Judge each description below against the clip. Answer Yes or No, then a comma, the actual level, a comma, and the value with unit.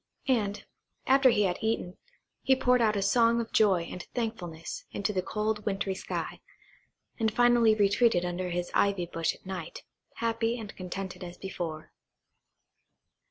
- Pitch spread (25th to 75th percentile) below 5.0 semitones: Yes, average, 4.0 semitones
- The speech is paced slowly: No, average, 150 wpm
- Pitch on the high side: Yes, high, 205 Hz